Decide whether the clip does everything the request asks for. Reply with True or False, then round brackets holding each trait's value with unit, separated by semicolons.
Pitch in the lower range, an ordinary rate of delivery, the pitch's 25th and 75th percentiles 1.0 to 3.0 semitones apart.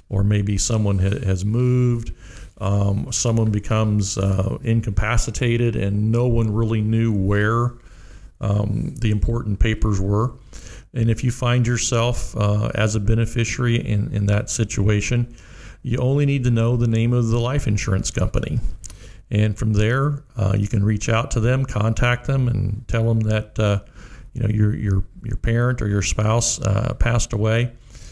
True (110 Hz; 160 wpm; 2.6 semitones)